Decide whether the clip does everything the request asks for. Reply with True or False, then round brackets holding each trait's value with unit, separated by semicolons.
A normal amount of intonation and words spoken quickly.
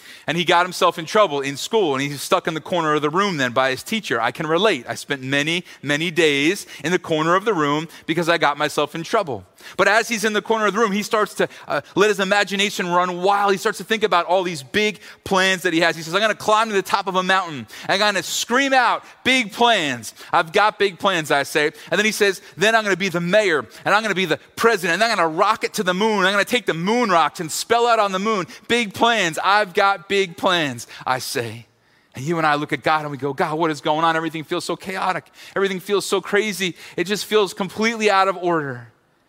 True (4.7 semitones; 265 wpm)